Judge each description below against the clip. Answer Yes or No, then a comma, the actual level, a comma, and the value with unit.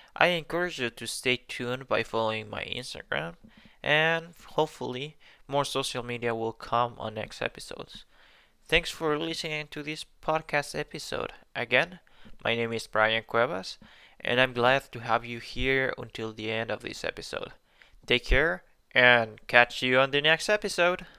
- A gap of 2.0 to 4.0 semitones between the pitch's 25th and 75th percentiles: No, average, 4.8 semitones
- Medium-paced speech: Yes, average, 155 wpm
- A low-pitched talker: Yes, low, 125 Hz